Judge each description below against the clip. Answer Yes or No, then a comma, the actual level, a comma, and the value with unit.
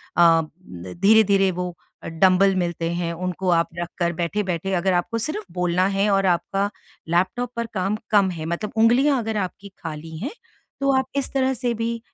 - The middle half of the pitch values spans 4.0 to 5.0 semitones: Yes, average, 4.3 semitones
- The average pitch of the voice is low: No, high, 190 Hz